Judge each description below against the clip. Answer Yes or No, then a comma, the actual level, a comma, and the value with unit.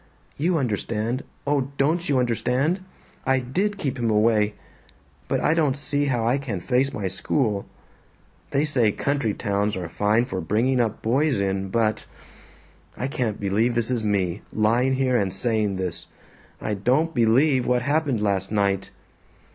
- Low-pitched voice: Yes, low, 120 Hz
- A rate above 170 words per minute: No, average, 155 wpm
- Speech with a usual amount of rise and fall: Yes, average, 4.7 semitones